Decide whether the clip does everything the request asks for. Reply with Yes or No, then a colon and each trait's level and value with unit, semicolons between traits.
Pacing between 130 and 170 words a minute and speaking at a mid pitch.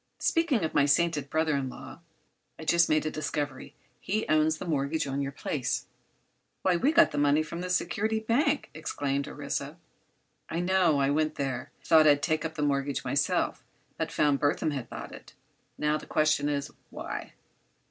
No: average, 180 wpm; medium, 155 Hz